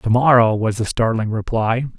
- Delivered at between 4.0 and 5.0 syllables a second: Yes, 4.8 syllables/s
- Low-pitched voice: Yes, low, 115 Hz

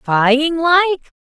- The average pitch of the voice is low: No, very high, 300 Hz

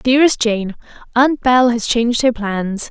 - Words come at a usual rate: Yes, average, 165 wpm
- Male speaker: No, female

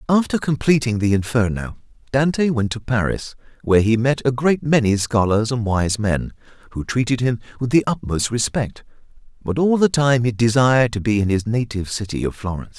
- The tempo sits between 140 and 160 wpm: No, average, 185 wpm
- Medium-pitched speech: No, low, 120 Hz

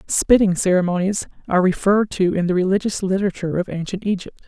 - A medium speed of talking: Yes, average, 160 wpm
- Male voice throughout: No, female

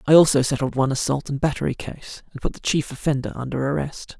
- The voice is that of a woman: No, male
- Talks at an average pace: No, fast, 215 wpm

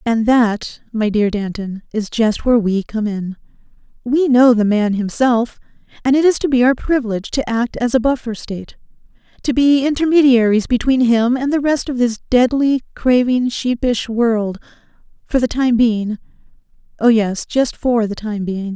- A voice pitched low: No, high, 235 Hz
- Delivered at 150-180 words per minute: Yes, average, 170 wpm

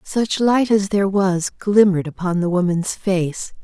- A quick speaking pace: No, average, 165 wpm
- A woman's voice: Yes, female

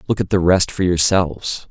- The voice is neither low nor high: No, very low, 90 Hz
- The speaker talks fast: Yes, fast, 210 wpm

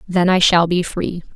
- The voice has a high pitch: No, medium, 175 Hz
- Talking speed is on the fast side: Yes, fast, 220 wpm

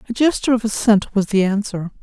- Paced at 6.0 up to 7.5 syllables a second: Yes, 6.3 syllables/s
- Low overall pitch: No, high, 215 Hz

